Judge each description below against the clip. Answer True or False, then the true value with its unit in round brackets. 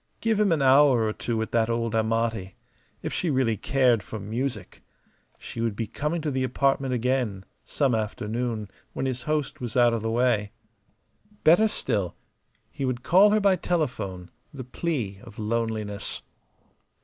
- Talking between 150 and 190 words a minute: True (160 wpm)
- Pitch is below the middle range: True (120 Hz)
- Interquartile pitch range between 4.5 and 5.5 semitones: False (3.9 semitones)